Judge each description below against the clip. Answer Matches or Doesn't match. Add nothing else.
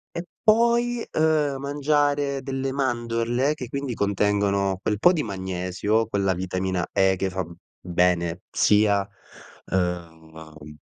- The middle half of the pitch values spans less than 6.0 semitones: Doesn't match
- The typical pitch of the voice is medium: Doesn't match